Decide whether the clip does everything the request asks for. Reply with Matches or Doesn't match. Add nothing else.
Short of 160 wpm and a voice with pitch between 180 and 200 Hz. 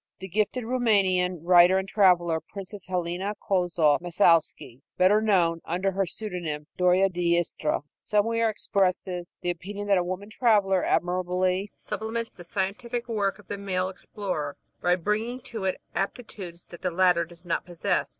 Matches